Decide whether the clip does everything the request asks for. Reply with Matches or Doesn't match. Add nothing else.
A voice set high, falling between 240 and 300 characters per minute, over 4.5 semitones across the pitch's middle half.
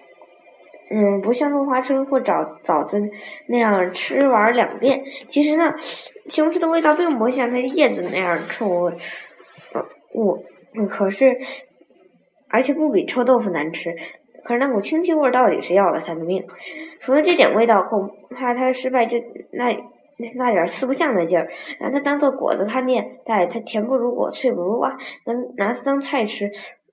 Matches